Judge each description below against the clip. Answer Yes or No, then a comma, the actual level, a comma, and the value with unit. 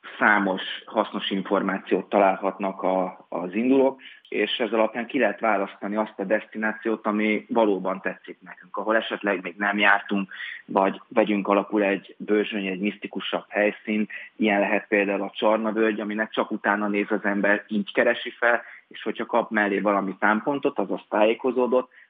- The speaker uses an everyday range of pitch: No, narrow, 1.4 semitones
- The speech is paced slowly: No, average, 150 wpm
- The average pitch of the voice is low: Yes, low, 105 Hz